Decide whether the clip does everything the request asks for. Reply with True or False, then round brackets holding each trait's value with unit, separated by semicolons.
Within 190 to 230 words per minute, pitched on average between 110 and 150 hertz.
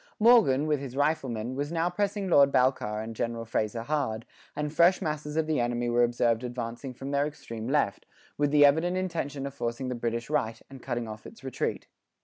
True (195 wpm; 135 Hz)